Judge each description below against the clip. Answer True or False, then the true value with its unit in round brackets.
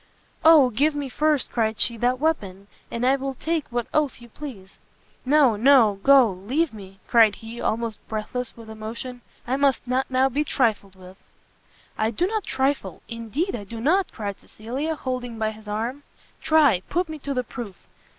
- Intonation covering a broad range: False (4.5 semitones)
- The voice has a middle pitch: False (245 Hz)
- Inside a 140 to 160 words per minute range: False (180 wpm)